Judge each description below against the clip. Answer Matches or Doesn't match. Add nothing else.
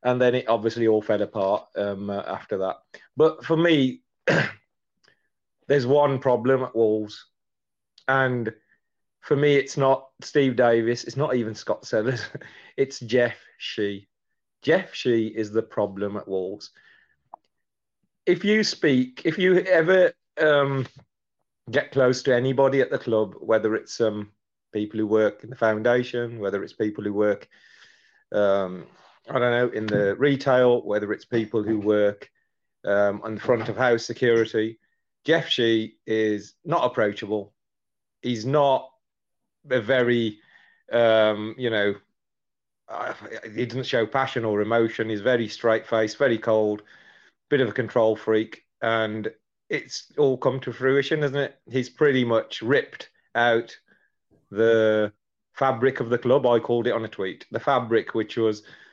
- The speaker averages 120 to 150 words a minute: Matches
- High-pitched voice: Doesn't match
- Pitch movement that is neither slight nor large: Matches